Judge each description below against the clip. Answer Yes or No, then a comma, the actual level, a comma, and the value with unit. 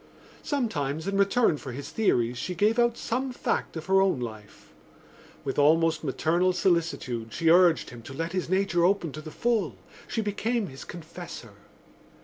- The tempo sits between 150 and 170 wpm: Yes, average, 165 wpm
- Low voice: No, medium, 170 Hz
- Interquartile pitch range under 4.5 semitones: No, wide, 5.5 semitones